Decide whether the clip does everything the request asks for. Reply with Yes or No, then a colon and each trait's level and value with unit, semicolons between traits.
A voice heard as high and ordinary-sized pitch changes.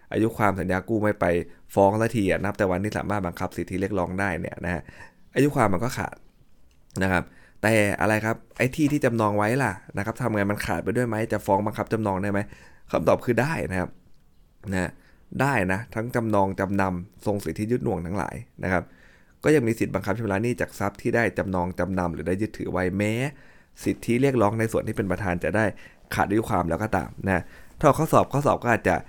No: low, 100 Hz; average, 3.6 semitones